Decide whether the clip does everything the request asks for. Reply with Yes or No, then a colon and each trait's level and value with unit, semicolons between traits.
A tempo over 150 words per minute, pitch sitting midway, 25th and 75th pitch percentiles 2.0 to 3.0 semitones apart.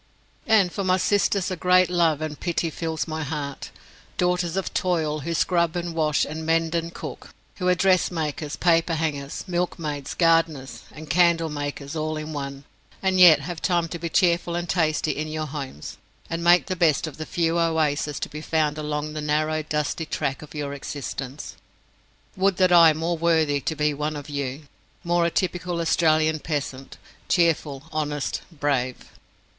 Yes: average, 170 wpm; medium, 160 Hz; narrow, 2.4 semitones